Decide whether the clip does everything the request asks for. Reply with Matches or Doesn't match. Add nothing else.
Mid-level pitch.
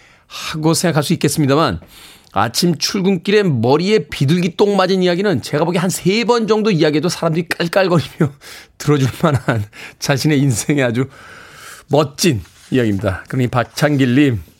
Matches